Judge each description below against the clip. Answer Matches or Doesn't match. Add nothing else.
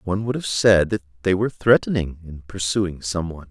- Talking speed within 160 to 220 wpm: Matches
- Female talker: Doesn't match